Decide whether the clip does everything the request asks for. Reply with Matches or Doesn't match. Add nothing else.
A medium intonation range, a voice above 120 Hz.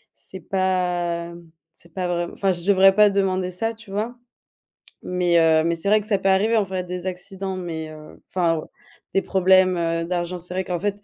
Doesn't match